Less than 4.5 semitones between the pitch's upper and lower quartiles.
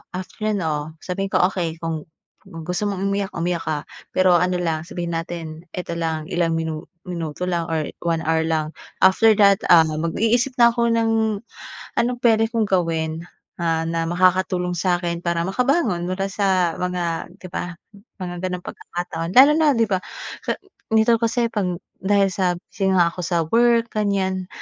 Yes: average, 3.4 semitones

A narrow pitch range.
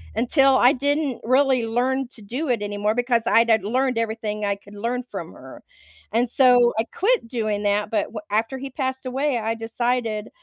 No: average, 3.0 semitones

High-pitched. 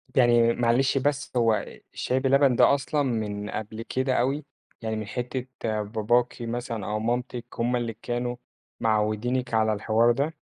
No: low, 120 Hz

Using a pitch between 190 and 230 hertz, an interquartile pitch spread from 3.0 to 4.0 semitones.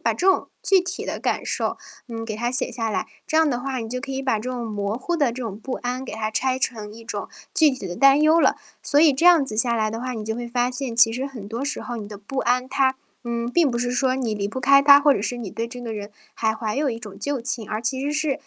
No: high, 245 Hz; average, 3.4 semitones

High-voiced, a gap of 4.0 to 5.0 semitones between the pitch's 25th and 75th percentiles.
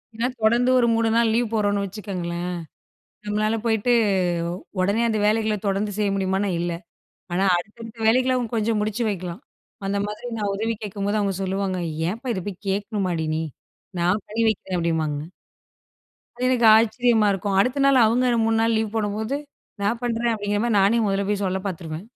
No: high, 210 Hz; average, 2.7 semitones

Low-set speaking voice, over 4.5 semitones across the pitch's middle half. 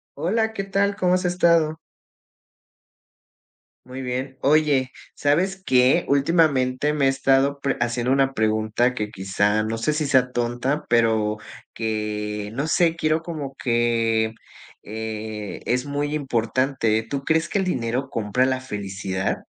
Yes: low, 130 Hz; average, 5.2 semitones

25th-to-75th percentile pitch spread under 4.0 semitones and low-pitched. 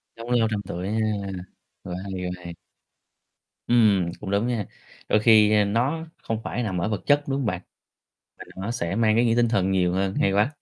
Yes: average, 3.5 semitones; low, 105 Hz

